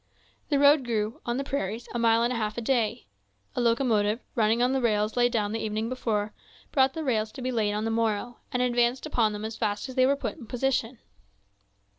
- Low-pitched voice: No, high, 235 Hz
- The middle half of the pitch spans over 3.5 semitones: No, average, 2.7 semitones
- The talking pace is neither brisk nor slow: No, fast, 225 wpm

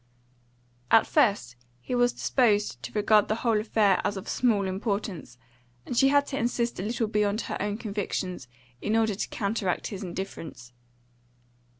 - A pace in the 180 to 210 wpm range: No, average, 160 wpm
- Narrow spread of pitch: No, average, 3.2 semitones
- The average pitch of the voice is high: Yes, high, 210 Hz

